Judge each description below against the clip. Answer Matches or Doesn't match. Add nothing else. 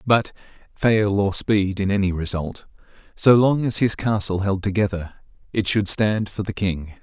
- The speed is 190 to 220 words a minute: Doesn't match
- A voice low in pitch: Matches